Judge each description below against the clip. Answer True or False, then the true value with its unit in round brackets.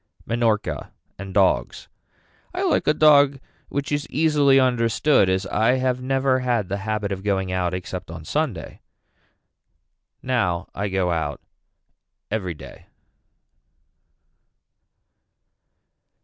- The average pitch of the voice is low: True (110 Hz)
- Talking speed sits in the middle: False (110 wpm)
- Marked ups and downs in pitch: True (5.9 semitones)